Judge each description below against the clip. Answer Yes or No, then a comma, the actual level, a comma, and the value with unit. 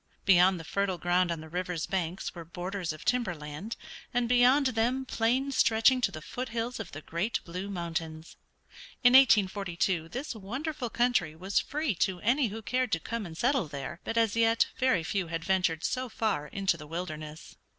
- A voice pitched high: Yes, high, 195 Hz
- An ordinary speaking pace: Yes, average, 185 wpm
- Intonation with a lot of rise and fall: Yes, wide, 6.2 semitones